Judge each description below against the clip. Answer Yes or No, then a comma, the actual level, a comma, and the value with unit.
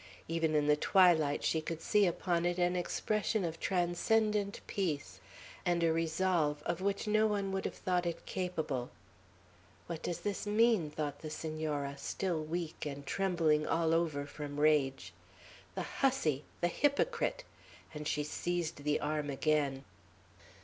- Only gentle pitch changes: No, average, 3.8 semitones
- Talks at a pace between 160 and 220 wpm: No, average, 150 wpm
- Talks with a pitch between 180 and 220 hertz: No, medium, 165 Hz